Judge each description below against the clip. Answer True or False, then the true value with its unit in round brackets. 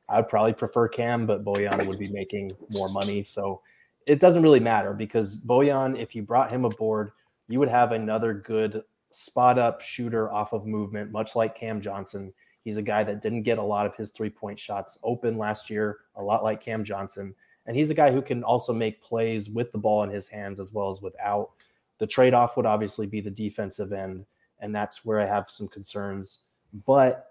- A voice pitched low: True (110 Hz)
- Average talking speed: False (210 wpm)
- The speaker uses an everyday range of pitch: False (2.2 semitones)